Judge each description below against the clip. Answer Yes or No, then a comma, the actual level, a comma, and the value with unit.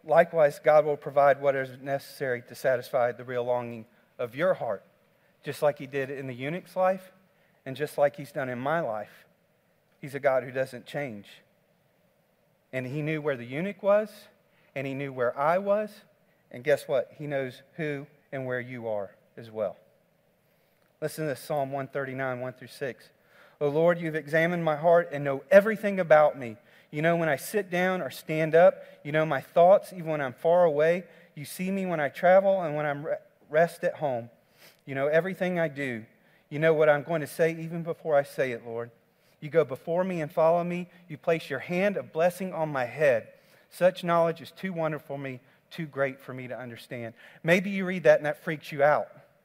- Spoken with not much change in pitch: No, average, 4.6 semitones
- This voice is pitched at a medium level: Yes, medium, 155 Hz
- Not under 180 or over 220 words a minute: Yes, average, 200 wpm